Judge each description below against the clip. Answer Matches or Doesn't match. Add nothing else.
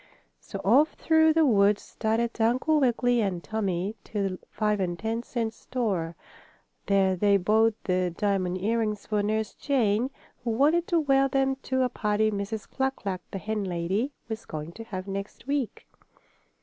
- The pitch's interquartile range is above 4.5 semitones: Doesn't match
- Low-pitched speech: Doesn't match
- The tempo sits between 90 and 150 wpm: Doesn't match